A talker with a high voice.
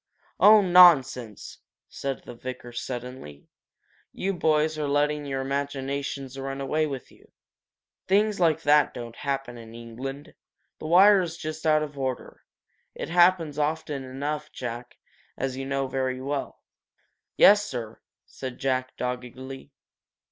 No: low, 135 Hz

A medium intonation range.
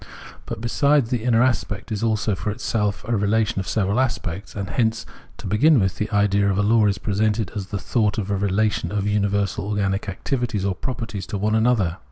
No: narrow, 2.2 semitones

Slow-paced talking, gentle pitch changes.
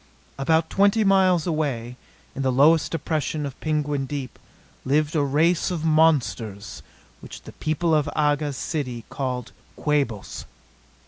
No: slow, 130 wpm; average, 3.1 semitones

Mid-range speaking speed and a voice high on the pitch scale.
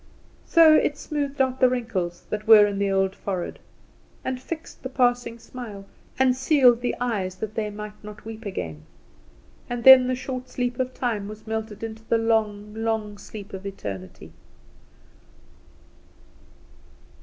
Yes: average, 150 wpm; high, 225 Hz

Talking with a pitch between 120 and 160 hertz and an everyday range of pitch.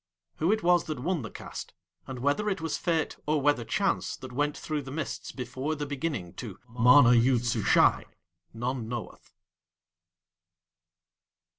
Yes: medium, 140 Hz; average, 4.4 semitones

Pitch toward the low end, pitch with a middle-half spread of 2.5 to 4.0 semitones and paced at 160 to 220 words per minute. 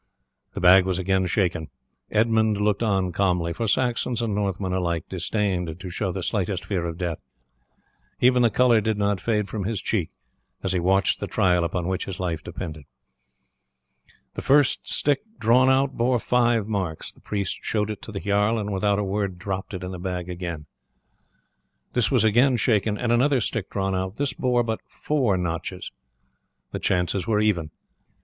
Yes: low, 100 Hz; average, 3.6 semitones; average, 180 wpm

